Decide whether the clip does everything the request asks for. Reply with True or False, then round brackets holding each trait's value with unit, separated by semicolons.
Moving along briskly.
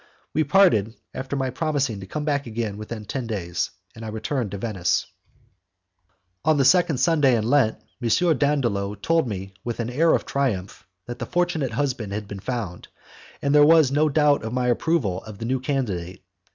False (190 wpm)